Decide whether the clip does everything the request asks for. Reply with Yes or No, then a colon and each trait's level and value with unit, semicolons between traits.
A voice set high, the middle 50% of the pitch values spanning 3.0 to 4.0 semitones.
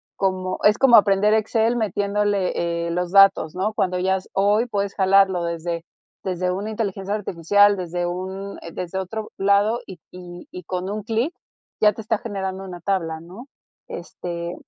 No: high, 195 Hz; narrow, 2.6 semitones